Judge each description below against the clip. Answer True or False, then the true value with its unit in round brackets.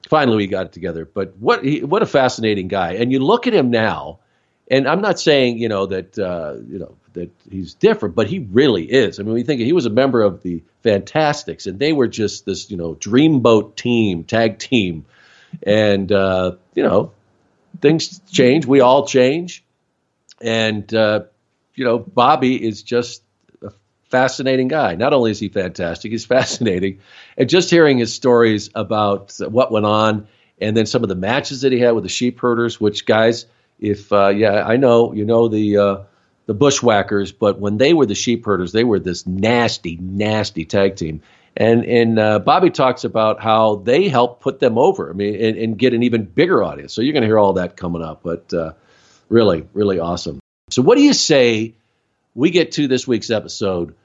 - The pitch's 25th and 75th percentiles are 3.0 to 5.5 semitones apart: True (3.5 semitones)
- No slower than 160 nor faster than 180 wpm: False (195 wpm)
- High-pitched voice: False (110 Hz)